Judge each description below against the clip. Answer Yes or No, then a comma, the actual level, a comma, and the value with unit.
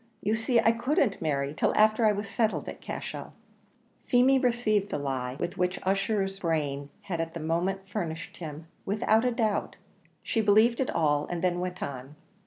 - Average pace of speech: Yes, average, 180 wpm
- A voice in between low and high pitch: No, high, 195 Hz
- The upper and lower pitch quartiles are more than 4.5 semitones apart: Yes, wide, 5.4 semitones